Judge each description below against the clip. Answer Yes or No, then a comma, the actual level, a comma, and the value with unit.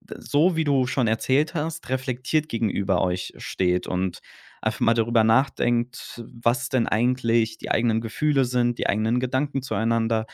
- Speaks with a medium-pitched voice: No, low, 120 Hz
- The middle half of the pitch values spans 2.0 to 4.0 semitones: Yes, average, 2.8 semitones